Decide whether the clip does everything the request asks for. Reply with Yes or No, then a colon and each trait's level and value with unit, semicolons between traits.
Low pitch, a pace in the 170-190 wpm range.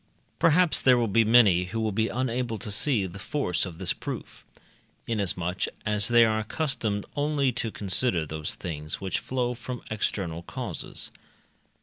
No: low, 110 Hz; average, 155 wpm